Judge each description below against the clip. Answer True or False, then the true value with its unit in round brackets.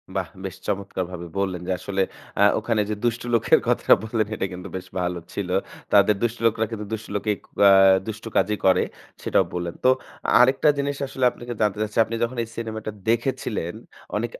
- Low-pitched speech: True (105 Hz)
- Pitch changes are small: False (3.3 semitones)